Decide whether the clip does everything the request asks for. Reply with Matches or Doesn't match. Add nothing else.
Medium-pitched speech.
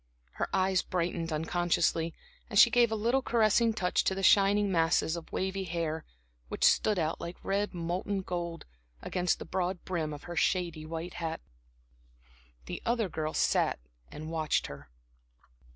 Matches